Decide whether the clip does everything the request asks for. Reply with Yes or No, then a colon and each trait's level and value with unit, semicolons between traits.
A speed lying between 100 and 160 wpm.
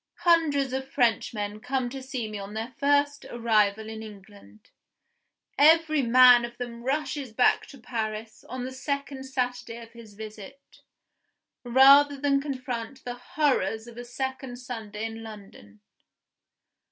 Yes: average, 140 wpm